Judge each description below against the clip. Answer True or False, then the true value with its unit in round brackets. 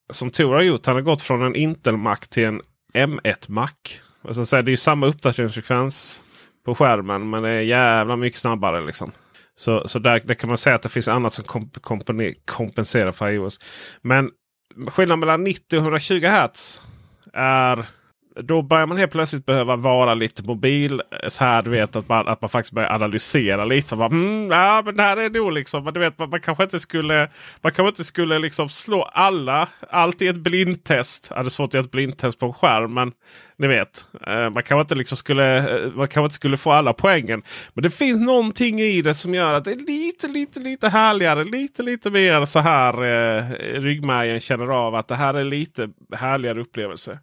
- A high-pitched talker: False (135 Hz)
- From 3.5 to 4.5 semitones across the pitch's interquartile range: False (5.6 semitones)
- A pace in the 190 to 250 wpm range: True (195 wpm)